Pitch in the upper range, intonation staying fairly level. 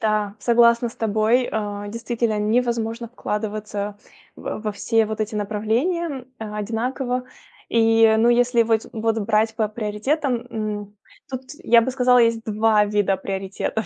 Yes: high, 220 Hz; narrow, 2.0 semitones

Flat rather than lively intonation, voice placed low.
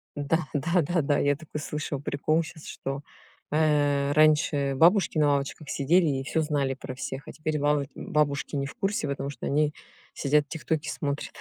No: narrow, 1.8 semitones; medium, 150 Hz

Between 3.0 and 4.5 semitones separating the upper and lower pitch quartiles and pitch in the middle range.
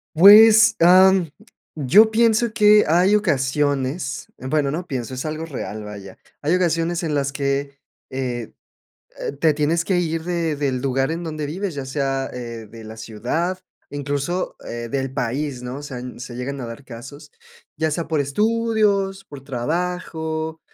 No: average, 5.0 semitones; medium, 150 Hz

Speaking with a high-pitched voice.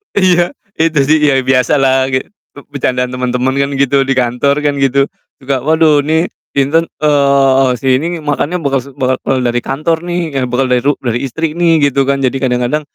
No: medium, 140 Hz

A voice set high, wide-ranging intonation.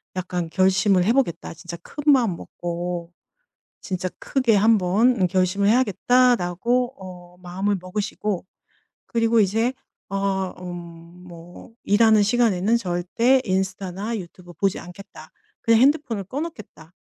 No: high, 195 Hz; average, 4.4 semitones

